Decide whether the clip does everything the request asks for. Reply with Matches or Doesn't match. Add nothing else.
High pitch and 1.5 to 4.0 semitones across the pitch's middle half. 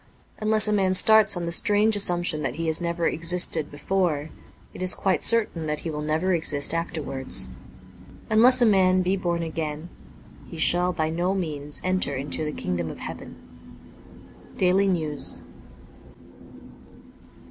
Doesn't match